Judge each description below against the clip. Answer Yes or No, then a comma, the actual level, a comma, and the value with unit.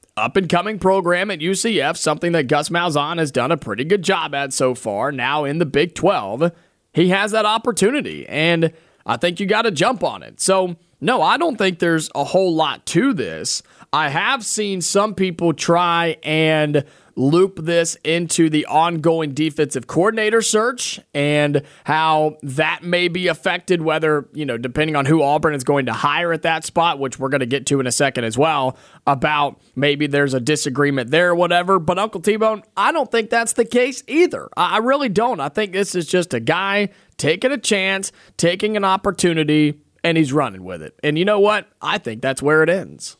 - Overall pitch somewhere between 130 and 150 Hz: No, medium, 170 Hz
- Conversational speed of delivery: Yes, average, 195 wpm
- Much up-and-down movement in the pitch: No, average, 4.6 semitones